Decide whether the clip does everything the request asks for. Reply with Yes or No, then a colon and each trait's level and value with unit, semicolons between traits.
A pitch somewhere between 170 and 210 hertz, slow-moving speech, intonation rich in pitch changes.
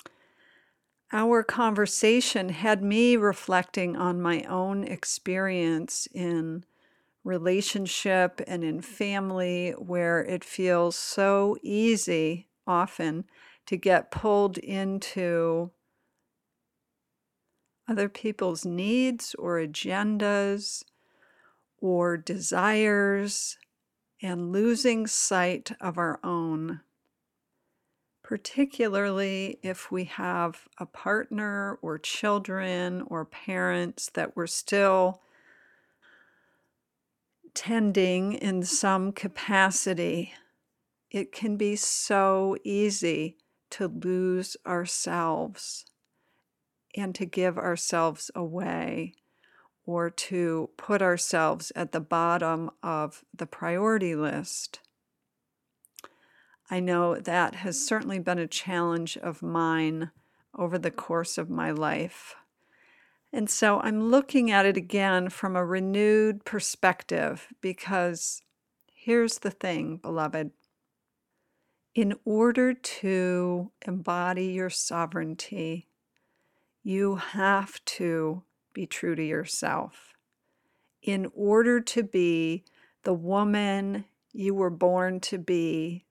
No: medium, 185 Hz; slow, 95 wpm; average, 2.9 semitones